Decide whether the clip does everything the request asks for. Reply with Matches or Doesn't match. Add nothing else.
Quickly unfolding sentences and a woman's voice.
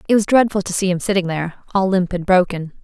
Matches